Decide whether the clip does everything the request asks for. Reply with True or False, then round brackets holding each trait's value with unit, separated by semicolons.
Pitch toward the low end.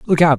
False (155 Hz)